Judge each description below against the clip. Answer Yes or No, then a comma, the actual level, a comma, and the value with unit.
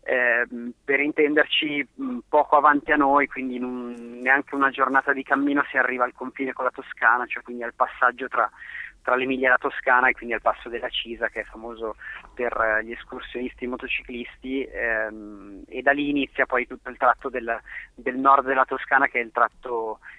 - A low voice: Yes, low, 130 Hz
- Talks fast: Yes, fast, 195 wpm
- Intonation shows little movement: Yes, narrow, 2.3 semitones